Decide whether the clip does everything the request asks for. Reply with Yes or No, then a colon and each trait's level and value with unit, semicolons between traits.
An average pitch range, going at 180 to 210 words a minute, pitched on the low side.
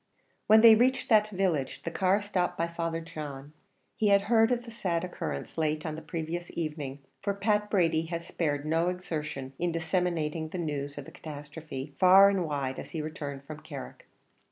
No: average, 4.0 semitones; average, 190 wpm; medium, 165 Hz